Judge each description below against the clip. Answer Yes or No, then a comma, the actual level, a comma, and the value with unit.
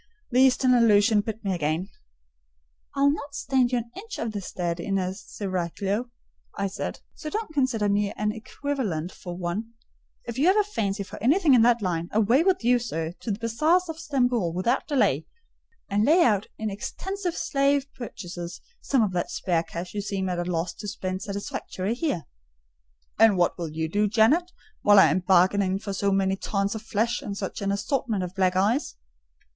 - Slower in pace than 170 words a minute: No, average, 190 wpm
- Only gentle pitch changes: No, average, 5.1 semitones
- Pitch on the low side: No, high, 210 Hz